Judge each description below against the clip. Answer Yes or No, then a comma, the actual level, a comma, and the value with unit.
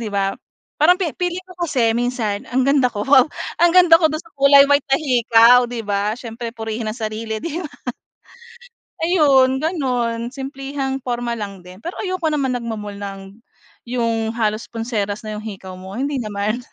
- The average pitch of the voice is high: Yes, high, 240 Hz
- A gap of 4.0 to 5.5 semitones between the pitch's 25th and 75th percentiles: Yes, average, 4.4 semitones